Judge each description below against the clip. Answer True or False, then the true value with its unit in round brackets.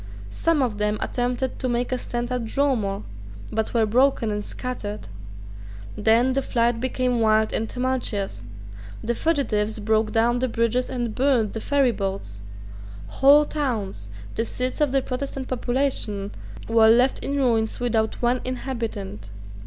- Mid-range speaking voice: False (240 Hz)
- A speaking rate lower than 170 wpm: True (145 wpm)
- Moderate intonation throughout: True (3.0 semitones)